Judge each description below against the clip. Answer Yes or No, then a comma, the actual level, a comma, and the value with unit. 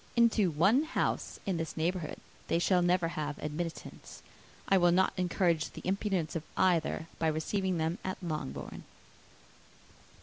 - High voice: No, medium, 175 Hz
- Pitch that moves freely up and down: No, average, 2.8 semitones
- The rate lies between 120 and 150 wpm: Yes, average, 140 wpm